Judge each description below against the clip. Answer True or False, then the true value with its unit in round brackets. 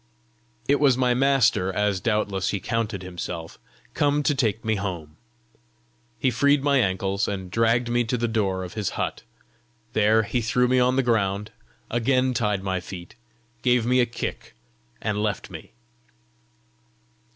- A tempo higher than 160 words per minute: False (155 wpm)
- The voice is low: True (110 Hz)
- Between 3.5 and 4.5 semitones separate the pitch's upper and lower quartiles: True (4.2 semitones)